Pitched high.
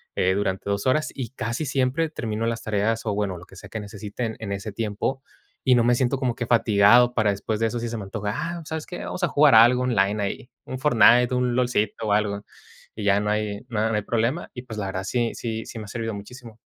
No: low, 115 Hz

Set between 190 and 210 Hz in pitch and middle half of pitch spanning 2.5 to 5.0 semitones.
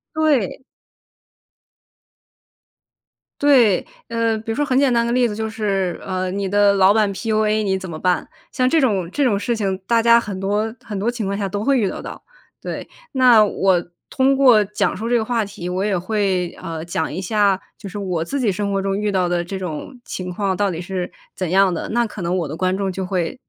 Yes: high, 200 Hz; average, 3.4 semitones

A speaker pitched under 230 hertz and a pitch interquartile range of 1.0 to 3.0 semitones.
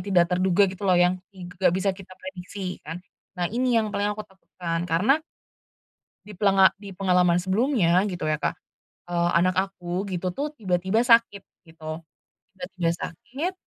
Yes: medium, 185 Hz; narrow, 2.5 semitones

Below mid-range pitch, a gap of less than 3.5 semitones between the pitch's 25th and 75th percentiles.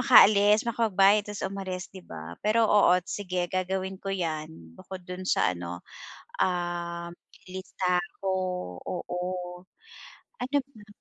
No: medium, 185 Hz; average, 2.7 semitones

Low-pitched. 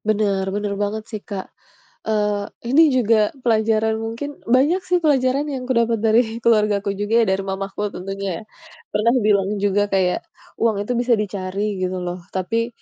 No: high, 215 Hz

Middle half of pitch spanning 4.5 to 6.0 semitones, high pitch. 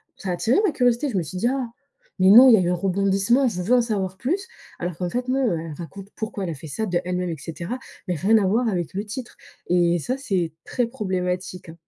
Yes: average, 5.1 semitones; high, 195 Hz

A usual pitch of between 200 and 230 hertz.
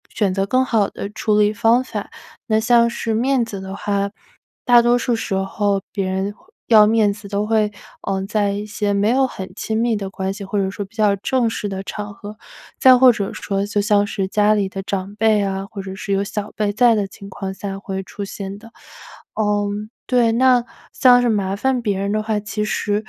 Yes: high, 210 Hz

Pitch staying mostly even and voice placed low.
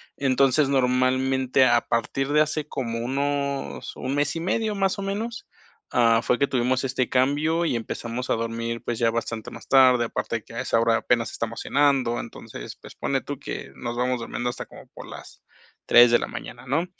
No: average, 3.2 semitones; low, 130 Hz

